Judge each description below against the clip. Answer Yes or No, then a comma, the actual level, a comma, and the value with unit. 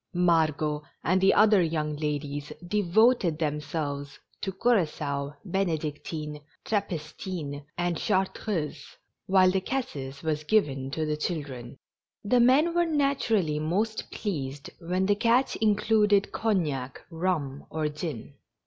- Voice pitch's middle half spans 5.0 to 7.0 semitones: Yes, wide, 5.5 semitones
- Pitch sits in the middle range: Yes, medium, 165 Hz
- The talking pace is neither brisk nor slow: No, slow, 120 wpm